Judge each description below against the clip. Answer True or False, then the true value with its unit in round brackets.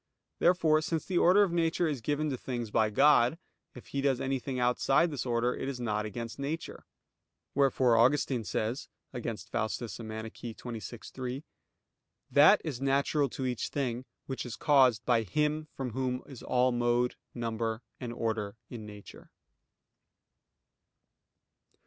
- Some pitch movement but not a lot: True (3.3 semitones)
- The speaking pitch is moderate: False (125 Hz)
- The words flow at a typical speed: True (145 wpm)